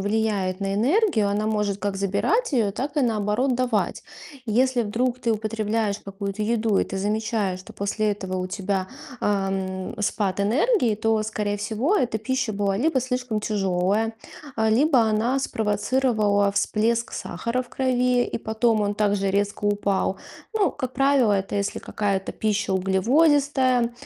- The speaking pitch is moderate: No, high, 215 Hz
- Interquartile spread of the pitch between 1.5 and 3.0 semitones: No, average, 3.6 semitones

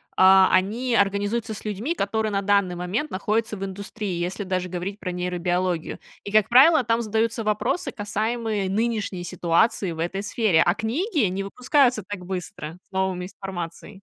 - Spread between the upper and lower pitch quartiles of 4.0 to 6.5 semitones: No, average, 3.3 semitones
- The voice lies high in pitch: Yes, high, 200 Hz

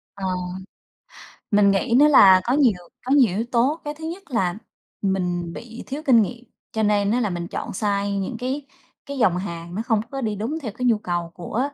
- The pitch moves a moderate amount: Yes, average, 5.0 semitones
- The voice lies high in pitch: Yes, high, 220 Hz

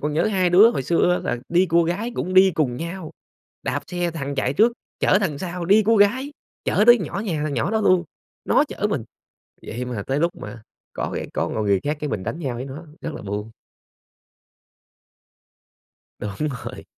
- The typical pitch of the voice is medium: Yes, medium, 170 Hz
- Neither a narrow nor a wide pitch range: No, wide, 5.9 semitones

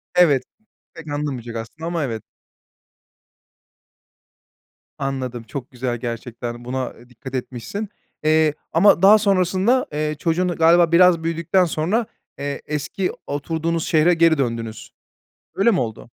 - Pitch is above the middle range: No, medium, 155 Hz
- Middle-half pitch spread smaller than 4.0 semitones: No, wide, 5.4 semitones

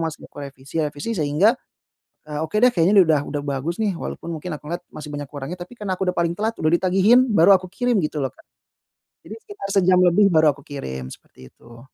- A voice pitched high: No, medium, 165 Hz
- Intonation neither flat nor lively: Yes, average, 4.8 semitones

